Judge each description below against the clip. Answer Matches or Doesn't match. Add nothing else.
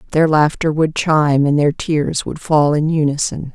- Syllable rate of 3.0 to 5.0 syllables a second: Matches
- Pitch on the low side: Doesn't match